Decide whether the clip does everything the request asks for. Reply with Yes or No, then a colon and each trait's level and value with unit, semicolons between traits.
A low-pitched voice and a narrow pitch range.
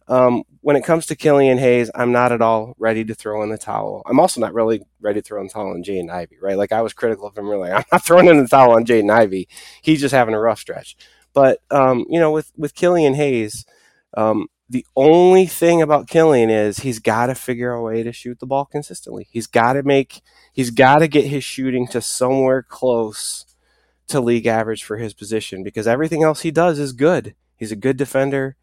No: low, 125 Hz; average, 4.1 semitones